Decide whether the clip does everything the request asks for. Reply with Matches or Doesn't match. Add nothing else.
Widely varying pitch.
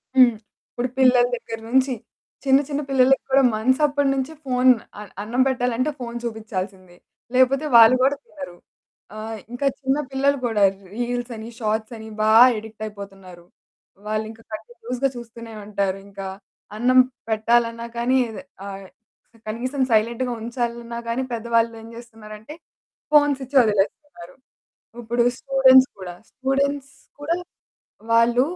Doesn't match